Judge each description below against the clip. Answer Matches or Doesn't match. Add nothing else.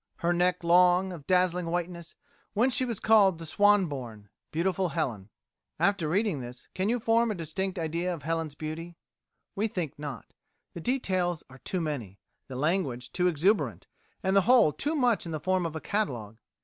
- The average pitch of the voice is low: Doesn't match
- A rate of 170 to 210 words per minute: Matches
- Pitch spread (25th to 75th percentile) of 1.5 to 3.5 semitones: Doesn't match